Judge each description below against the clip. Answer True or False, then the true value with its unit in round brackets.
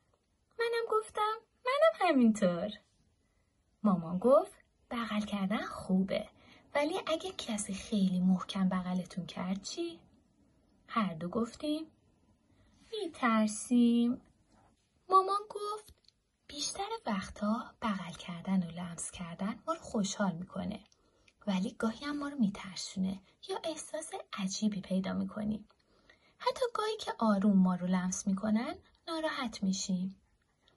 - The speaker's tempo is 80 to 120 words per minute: True (105 wpm)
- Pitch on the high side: True (215 Hz)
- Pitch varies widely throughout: True (8.6 semitones)